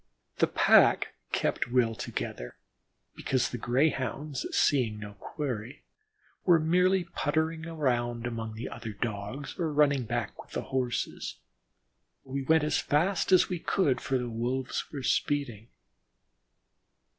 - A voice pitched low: Yes, low, 130 Hz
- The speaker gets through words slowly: Yes, slow, 130 wpm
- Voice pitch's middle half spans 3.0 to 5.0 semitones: Yes, average, 4.5 semitones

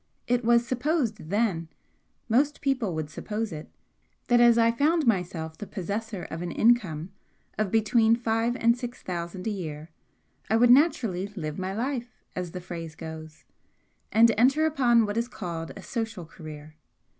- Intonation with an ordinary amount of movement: No, wide, 5.7 semitones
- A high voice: Yes, high, 220 Hz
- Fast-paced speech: No, average, 160 wpm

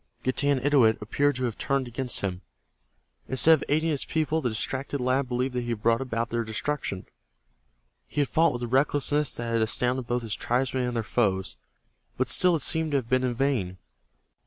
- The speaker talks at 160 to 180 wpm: No, average, 195 wpm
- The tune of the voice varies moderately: Yes, average, 3.4 semitones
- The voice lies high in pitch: No, low, 130 Hz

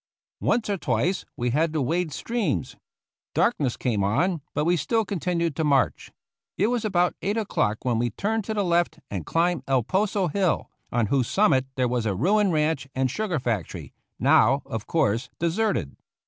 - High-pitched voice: No, medium, 160 Hz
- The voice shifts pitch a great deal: Yes, wide, 7.5 semitones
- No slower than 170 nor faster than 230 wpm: Yes, average, 180 wpm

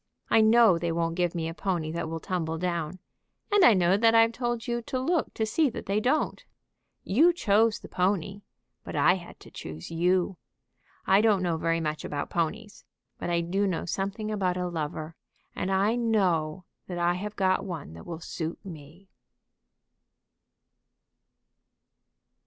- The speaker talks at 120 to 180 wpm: Yes, average, 170 wpm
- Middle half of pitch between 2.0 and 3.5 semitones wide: No, average, 4.5 semitones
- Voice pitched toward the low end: No, medium, 185 Hz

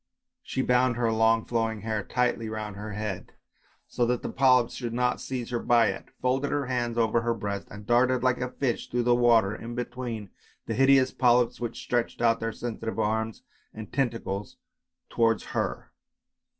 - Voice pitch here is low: Yes, low, 120 Hz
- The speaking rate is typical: Yes, average, 175 wpm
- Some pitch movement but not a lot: No, narrow, 1.9 semitones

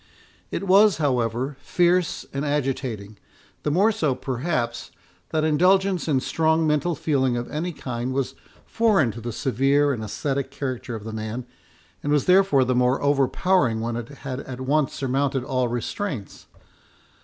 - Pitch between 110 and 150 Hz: Yes, low, 135 Hz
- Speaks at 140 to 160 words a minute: Yes, average, 155 wpm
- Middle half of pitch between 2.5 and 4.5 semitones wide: Yes, average, 4.2 semitones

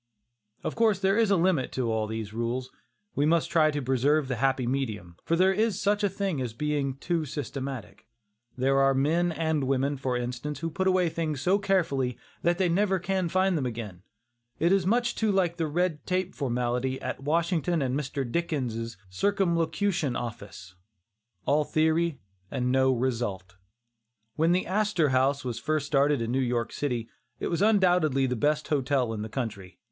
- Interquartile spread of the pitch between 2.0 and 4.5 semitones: No, wide, 5.6 semitones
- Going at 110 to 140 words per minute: No, average, 180 wpm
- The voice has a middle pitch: Yes, medium, 145 Hz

